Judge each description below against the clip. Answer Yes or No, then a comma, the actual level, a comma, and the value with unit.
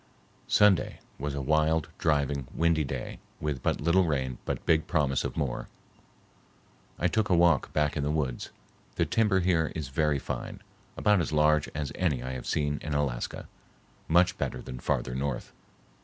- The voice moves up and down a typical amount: Yes, average, 3.2 semitones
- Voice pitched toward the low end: Yes, very low, 75 Hz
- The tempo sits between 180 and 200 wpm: No, average, 170 wpm